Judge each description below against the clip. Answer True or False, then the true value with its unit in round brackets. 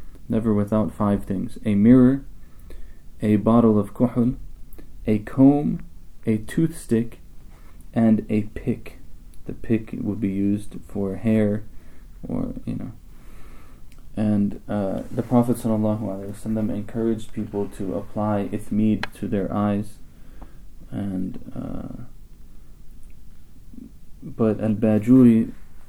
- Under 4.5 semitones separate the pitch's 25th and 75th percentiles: True (3.1 semitones)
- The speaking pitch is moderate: False (105 Hz)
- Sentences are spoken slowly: True (110 wpm)